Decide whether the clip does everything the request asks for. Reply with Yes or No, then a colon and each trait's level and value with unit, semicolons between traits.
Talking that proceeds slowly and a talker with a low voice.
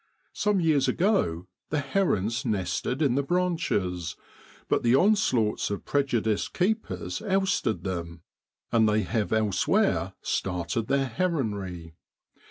Yes: slow, 115 wpm; low, 115 Hz